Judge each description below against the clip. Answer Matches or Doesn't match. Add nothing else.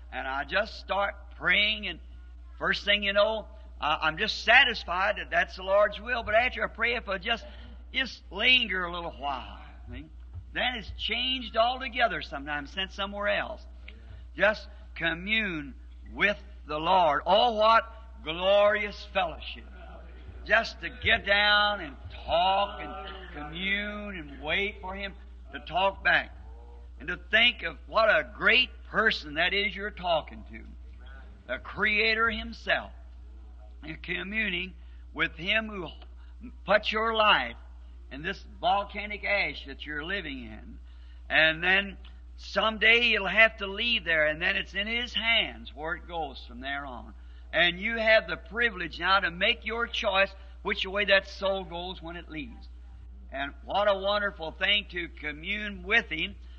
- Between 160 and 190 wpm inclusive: Doesn't match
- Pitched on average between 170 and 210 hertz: Matches